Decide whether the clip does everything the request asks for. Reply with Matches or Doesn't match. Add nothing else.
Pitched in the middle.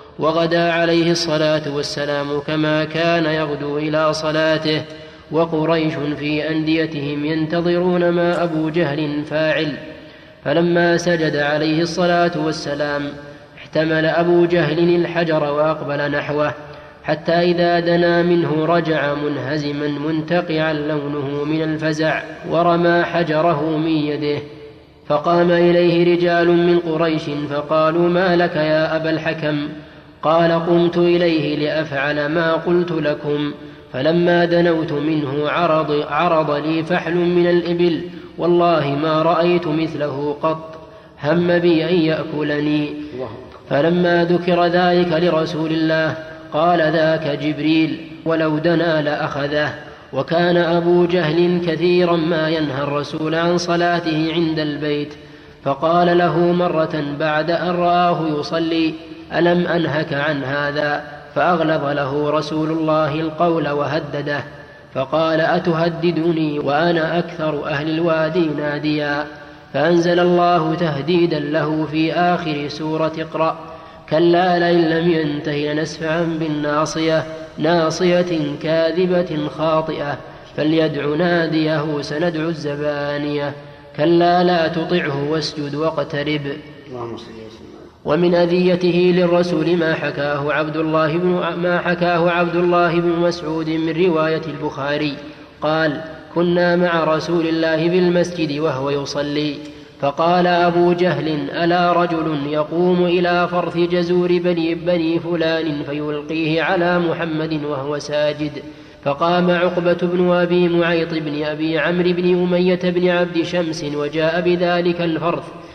Matches